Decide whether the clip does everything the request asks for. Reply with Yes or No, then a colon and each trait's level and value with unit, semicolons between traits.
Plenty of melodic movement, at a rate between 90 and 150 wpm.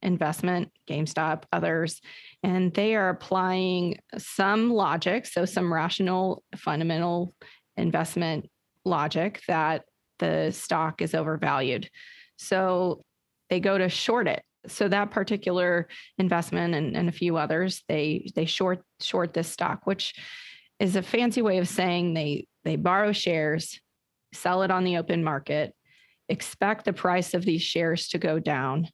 No: average, 2.7 semitones; average, 140 wpm